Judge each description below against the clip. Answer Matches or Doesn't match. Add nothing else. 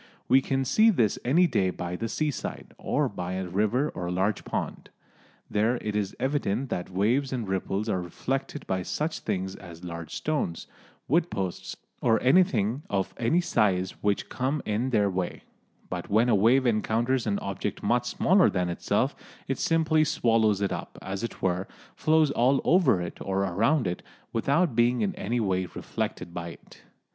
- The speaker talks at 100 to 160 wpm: Doesn't match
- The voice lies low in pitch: Matches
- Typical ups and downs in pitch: Doesn't match